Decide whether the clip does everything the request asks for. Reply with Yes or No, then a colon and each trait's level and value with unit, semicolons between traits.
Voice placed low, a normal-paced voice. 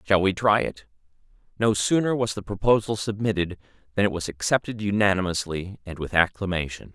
Yes: low, 100 Hz; average, 155 wpm